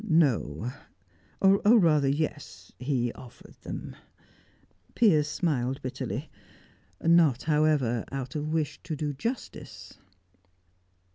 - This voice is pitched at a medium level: Yes, medium, 150 Hz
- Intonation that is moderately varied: Yes, average, 3.8 semitones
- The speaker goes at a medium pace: No, slow, 95 wpm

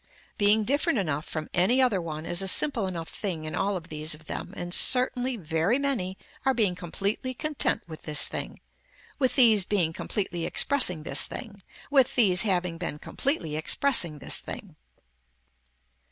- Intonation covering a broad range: Yes, wide, 7.1 semitones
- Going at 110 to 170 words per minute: Yes, average, 165 wpm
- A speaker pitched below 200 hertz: Yes, high, 190 Hz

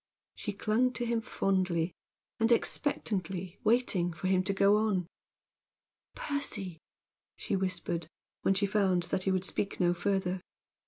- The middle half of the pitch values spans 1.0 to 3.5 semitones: Yes, average, 2.9 semitones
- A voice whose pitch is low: No, high, 195 Hz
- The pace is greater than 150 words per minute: No, average, 140 wpm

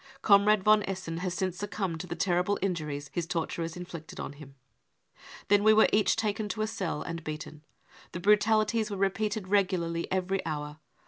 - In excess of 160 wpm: Yes, average, 180 wpm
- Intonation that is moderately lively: Yes, average, 3.8 semitones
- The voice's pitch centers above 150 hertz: Yes, medium, 185 Hz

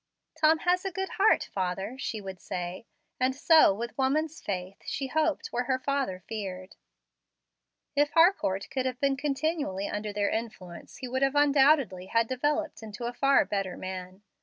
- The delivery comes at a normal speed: Yes, average, 160 wpm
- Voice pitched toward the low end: No, very high, 255 Hz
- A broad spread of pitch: Yes, wide, 6.8 semitones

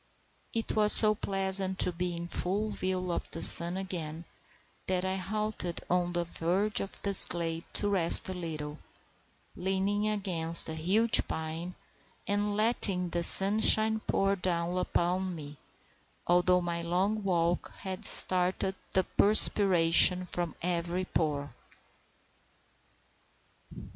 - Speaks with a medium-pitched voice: Yes, medium, 180 Hz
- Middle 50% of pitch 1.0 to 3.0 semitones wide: Yes, narrow, 2.5 semitones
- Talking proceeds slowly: Yes, slow, 125 wpm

